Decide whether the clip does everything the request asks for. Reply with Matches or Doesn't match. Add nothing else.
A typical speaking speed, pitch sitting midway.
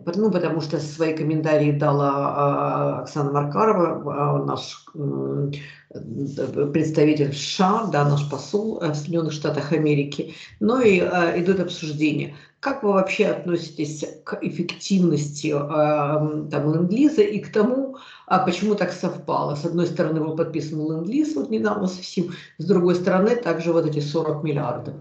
Matches